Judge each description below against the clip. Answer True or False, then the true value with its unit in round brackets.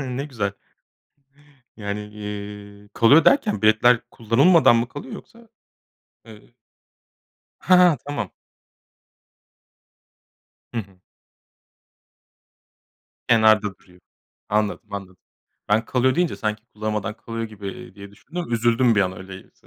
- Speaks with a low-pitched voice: True (110 Hz)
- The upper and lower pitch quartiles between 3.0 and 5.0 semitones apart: True (3.7 semitones)